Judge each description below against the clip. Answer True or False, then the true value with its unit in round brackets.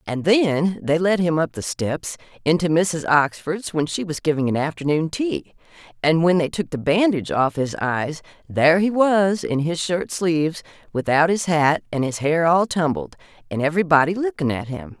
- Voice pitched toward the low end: False (165 Hz)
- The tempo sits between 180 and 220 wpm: True (190 wpm)